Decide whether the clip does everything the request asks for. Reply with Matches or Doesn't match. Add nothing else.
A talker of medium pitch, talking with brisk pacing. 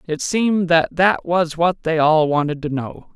Matches